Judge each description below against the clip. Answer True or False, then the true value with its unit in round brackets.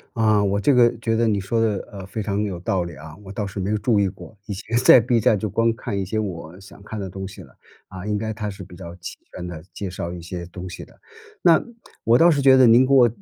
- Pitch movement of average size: True (3.4 semitones)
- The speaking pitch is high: False (100 Hz)